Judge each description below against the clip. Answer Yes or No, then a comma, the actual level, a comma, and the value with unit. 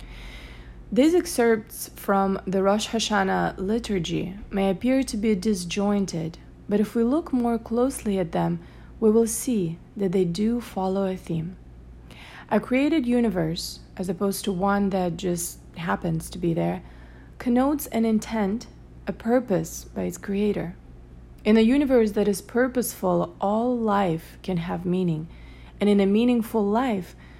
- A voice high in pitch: Yes, high, 200 Hz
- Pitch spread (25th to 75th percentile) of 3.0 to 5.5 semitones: Yes, average, 4.6 semitones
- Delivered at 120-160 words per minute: Yes, average, 145 wpm